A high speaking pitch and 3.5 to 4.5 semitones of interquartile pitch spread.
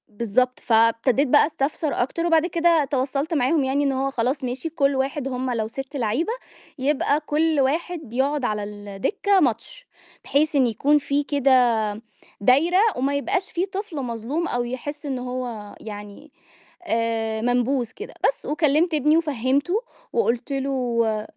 Yes: very high, 270 Hz; average, 3.9 semitones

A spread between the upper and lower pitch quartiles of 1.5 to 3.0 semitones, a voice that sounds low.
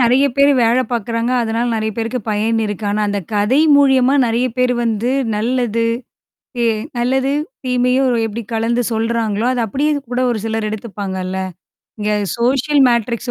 No: narrow, 2.5 semitones; high, 235 Hz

